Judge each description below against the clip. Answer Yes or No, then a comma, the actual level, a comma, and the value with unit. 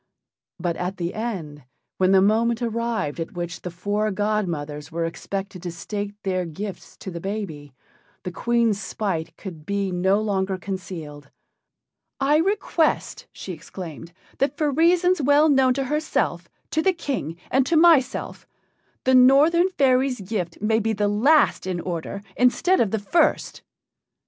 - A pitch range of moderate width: No, wide, 6.6 semitones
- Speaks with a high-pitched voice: Yes, high, 205 Hz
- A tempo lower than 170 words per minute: Yes, average, 150 wpm